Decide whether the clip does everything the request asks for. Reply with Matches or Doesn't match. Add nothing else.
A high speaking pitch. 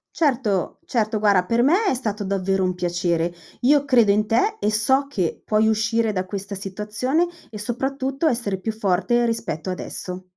Matches